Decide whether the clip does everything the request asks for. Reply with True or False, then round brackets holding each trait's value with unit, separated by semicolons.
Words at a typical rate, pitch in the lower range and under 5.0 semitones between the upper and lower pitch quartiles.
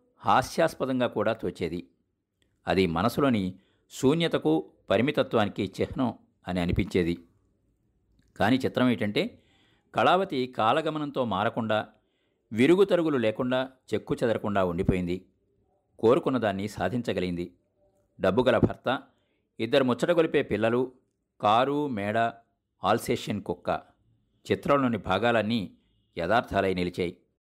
False (85 wpm; 110 Hz; 5.4 semitones)